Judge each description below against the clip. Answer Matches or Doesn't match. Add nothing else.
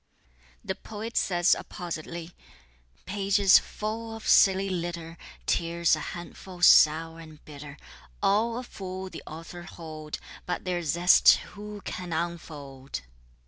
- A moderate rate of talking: Doesn't match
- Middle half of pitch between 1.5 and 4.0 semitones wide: Matches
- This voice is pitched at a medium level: Matches